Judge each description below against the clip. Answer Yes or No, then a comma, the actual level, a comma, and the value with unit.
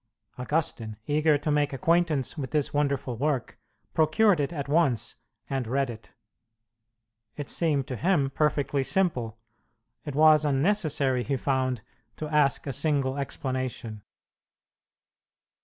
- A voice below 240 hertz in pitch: Yes, medium, 140 Hz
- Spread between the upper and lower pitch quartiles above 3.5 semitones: No, average, 2.8 semitones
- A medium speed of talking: No, slow, 125 wpm